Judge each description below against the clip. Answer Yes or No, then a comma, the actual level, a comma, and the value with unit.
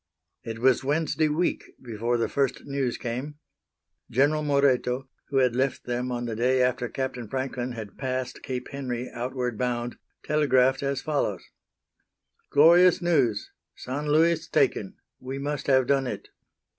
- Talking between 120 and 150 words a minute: Yes, average, 145 wpm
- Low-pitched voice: Yes, low, 130 Hz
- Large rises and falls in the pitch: No, narrow, 2.5 semitones